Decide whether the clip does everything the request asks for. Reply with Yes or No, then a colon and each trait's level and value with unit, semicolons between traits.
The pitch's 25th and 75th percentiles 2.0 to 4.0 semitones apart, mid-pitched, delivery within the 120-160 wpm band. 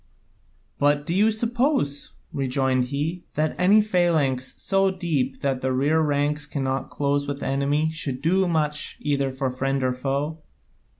Yes: average, 3.6 semitones; medium, 145 Hz; average, 155 wpm